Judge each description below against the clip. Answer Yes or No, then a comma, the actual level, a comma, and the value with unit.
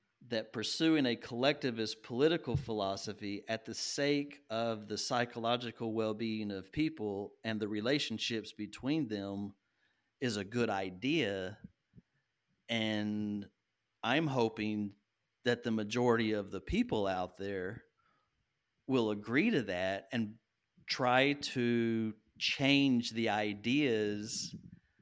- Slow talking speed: Yes, slow, 110 wpm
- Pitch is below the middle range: Yes, low, 110 Hz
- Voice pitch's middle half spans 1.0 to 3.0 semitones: Yes, narrow, 2.6 semitones